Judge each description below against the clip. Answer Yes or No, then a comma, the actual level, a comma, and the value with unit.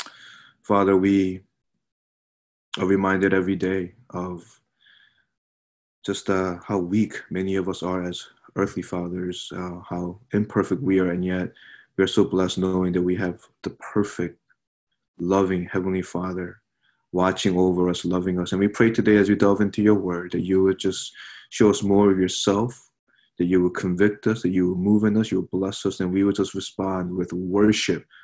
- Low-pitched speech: Yes, very low, 95 Hz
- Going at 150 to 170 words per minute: No, average, 180 wpm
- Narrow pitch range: Yes, narrow, 1.8 semitones